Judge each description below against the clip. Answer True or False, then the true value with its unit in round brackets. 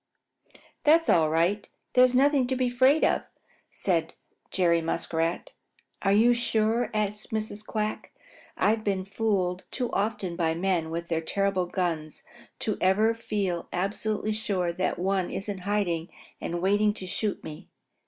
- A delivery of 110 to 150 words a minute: True (145 wpm)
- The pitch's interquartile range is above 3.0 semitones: True (3.8 semitones)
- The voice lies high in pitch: True (200 Hz)